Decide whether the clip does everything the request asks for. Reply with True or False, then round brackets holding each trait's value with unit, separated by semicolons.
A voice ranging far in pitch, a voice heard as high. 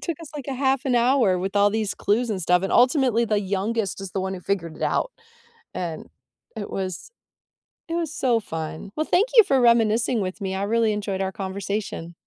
False (4.7 semitones; 210 Hz)